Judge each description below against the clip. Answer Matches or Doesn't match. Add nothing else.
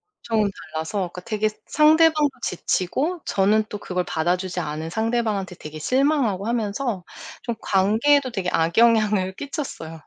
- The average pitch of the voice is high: Matches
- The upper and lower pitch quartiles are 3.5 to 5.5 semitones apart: Matches